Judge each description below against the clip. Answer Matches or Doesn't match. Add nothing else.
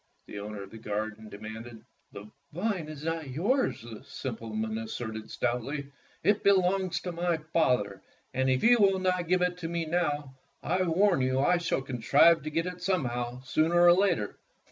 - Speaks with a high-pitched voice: Doesn't match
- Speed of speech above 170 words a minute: Matches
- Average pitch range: Doesn't match